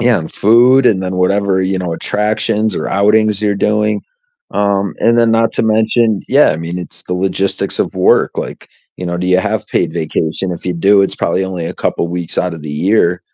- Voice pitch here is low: Yes, very low, 95 Hz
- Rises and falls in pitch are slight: No, average, 3.2 semitones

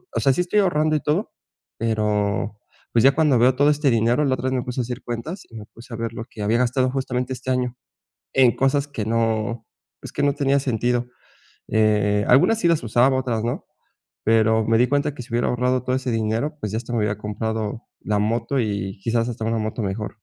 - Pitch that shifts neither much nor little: Yes, average, 3.1 semitones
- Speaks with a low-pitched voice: Yes, low, 120 Hz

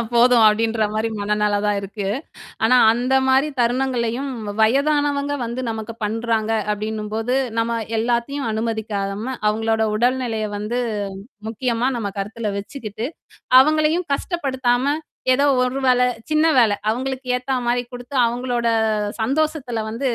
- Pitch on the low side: No, high, 235 Hz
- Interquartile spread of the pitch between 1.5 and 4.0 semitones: Yes, average, 3.1 semitones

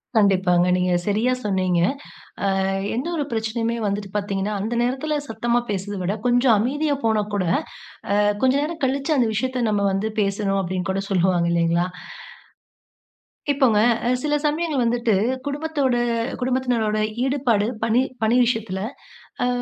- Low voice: No, high, 220 Hz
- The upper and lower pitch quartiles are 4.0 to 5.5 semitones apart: Yes, average, 4.6 semitones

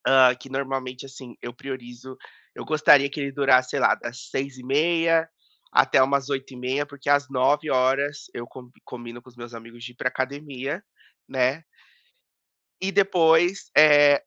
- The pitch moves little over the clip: Yes, narrow, 2.3 semitones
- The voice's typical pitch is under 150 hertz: Yes, low, 135 Hz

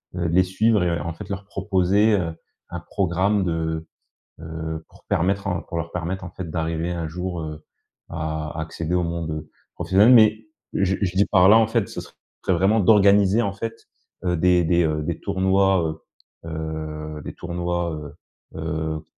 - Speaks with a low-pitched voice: Yes, very low, 90 Hz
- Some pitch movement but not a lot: Yes, average, 3.3 semitones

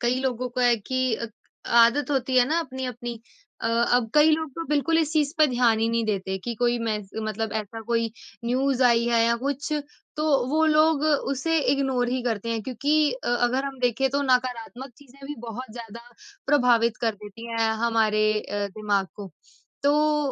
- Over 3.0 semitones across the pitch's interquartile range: Yes, average, 3.4 semitones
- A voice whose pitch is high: Yes, high, 245 Hz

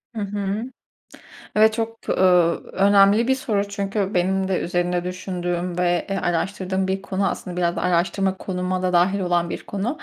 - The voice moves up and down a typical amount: No, narrow, 2.1 semitones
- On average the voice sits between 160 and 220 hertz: Yes, high, 190 Hz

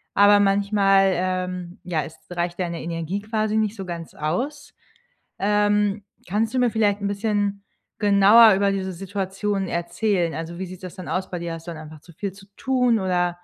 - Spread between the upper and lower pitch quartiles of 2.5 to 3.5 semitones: Yes, average, 2.8 semitones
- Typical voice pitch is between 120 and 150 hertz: No, high, 195 Hz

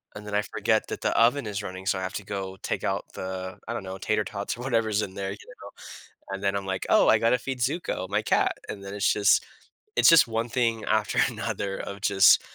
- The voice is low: Yes, low, 105 Hz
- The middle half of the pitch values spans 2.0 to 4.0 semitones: Yes, average, 2.7 semitones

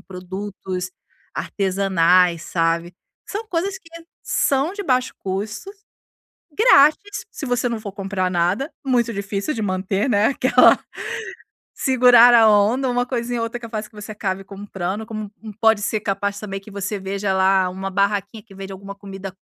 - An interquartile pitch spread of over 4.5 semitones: No, average, 3.9 semitones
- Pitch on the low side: No, high, 205 Hz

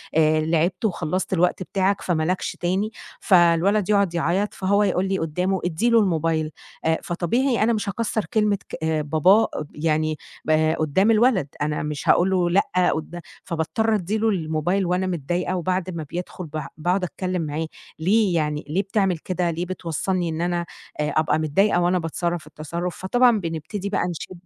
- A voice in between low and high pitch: Yes, medium, 175 Hz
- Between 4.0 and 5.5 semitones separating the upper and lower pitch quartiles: No, average, 3.4 semitones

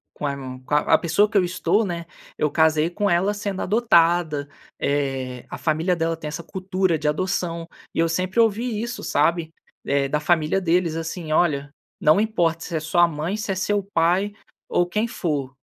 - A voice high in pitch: No, medium, 170 Hz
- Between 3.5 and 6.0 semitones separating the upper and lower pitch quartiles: Yes, average, 3.8 semitones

